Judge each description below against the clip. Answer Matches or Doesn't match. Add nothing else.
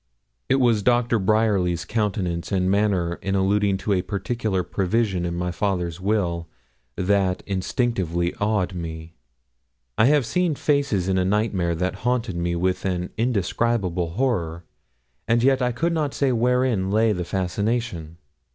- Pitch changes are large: Doesn't match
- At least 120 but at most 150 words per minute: Matches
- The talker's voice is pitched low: Matches